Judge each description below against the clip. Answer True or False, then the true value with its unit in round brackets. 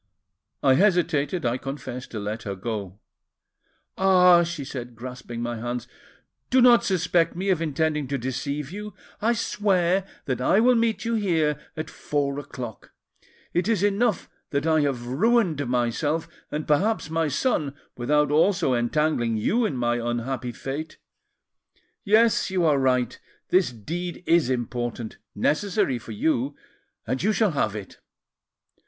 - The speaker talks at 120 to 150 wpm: True (145 wpm)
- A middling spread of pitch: False (6.7 semitones)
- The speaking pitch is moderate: True (150 Hz)